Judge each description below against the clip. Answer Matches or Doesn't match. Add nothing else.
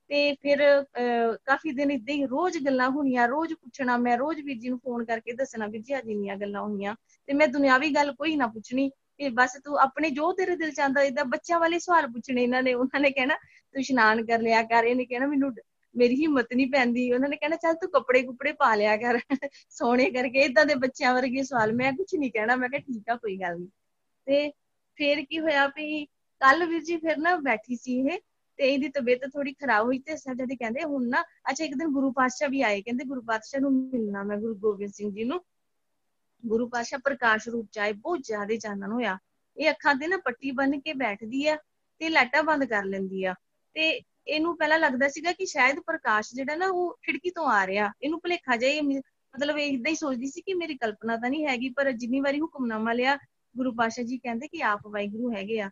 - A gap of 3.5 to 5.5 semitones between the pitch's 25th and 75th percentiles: Matches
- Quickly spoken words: Matches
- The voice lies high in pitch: Matches